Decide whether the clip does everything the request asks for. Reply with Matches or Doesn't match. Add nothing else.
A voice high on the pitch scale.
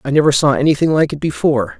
Doesn't match